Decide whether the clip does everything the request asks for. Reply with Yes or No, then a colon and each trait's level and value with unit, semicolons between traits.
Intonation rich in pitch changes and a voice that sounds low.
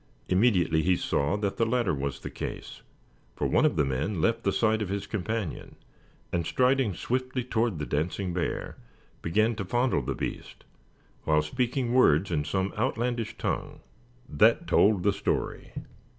Yes: wide, 5.9 semitones; low, 100 Hz